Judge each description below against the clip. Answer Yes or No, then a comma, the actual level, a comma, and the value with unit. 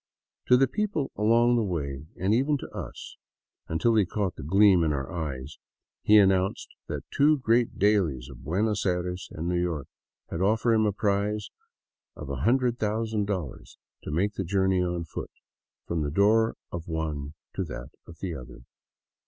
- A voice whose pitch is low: Yes, very low, 95 Hz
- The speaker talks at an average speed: Yes, average, 170 wpm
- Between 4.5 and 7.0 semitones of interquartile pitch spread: Yes, average, 5.2 semitones